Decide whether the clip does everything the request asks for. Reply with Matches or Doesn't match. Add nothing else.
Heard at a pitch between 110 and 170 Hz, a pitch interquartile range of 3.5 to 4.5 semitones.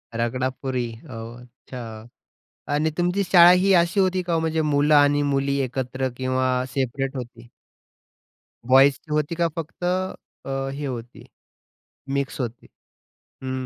Matches